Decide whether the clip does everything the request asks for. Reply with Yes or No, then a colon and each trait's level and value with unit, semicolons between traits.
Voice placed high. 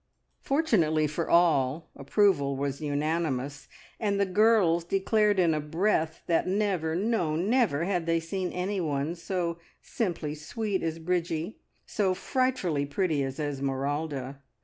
No: medium, 165 Hz